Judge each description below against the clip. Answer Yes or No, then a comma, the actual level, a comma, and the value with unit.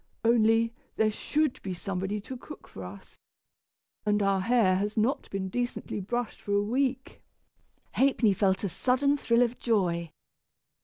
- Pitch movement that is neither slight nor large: Yes, average, 4.1 semitones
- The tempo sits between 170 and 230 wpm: No, average, 150 wpm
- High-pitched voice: Yes, high, 215 Hz